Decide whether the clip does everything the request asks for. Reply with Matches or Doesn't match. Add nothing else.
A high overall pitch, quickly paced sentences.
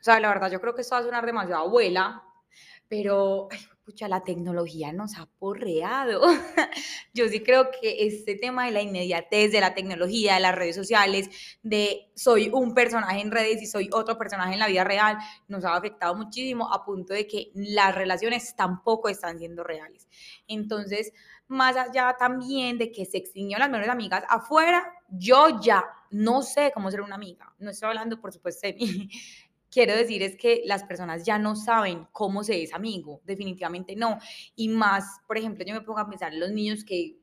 Matches